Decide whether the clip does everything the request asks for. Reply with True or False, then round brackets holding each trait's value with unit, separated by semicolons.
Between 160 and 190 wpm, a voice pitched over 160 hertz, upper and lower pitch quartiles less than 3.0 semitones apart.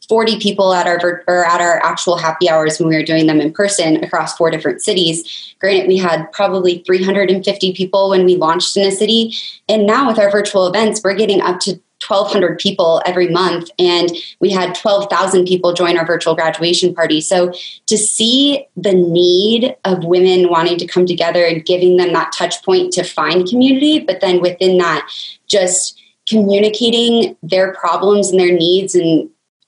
True (180 wpm; 185 Hz; 2.5 semitones)